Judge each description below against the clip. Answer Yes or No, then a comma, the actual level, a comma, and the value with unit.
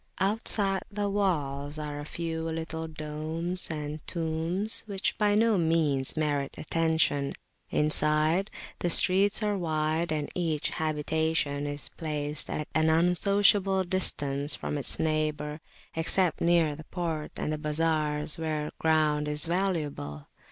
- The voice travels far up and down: No, average, 2.7 semitones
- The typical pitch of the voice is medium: Yes, medium, 160 Hz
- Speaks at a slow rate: Yes, slow, 130 wpm